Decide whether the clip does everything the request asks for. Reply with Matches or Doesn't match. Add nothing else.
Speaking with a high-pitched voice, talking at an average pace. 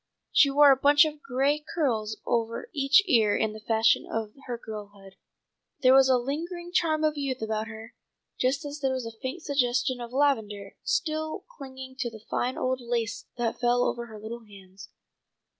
Matches